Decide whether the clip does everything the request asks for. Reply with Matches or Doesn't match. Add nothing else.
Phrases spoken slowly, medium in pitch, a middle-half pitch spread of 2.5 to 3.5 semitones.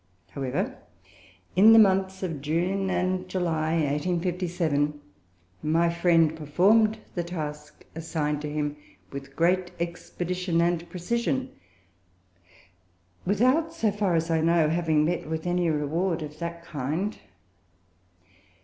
Matches